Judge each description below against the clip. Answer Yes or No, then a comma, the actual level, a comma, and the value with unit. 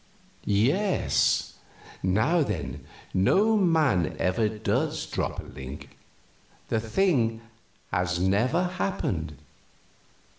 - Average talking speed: No, slow, 85 wpm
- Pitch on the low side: Yes, low, 110 Hz